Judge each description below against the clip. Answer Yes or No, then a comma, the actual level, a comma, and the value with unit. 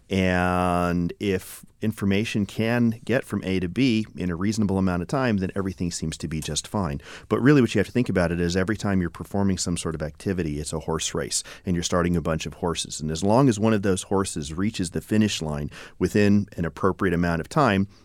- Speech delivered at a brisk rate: Yes, fast, 230 wpm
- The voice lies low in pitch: Yes, very low, 95 Hz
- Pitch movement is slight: No, average, 3.4 semitones